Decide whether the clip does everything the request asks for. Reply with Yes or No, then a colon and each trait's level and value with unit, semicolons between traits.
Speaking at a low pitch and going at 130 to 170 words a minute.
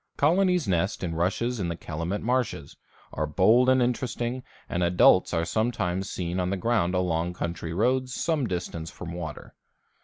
Yes: very low, 95 Hz; average, 160 wpm